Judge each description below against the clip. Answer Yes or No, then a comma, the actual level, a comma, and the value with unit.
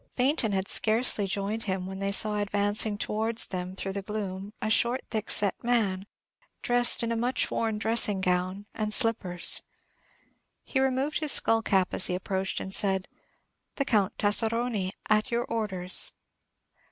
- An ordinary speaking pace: Yes, average, 155 wpm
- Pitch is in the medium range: No, high, 210 Hz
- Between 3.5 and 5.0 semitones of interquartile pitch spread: No, average, 3.1 semitones